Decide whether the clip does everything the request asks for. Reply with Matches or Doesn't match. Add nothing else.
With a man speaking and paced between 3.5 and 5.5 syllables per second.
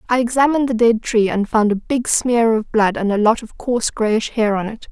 Doesn't match